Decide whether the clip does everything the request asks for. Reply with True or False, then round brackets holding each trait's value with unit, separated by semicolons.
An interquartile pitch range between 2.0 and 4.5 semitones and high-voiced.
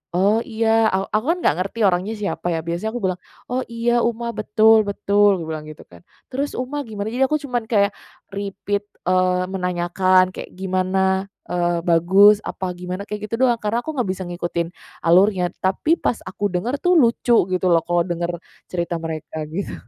True (3.8 semitones; 195 Hz)